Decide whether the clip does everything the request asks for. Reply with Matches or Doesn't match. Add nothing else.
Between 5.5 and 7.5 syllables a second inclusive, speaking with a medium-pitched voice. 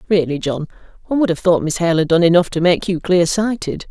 Matches